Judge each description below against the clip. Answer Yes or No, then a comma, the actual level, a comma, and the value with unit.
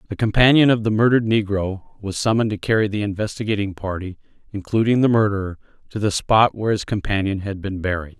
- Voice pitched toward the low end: Yes, low, 105 Hz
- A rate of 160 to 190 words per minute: Yes, average, 185 wpm